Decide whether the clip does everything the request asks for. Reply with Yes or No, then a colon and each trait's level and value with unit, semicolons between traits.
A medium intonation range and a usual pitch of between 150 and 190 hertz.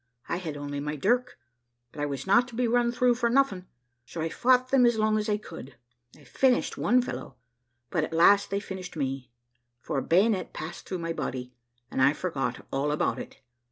No: wide, 8.3 semitones; medium, 185 Hz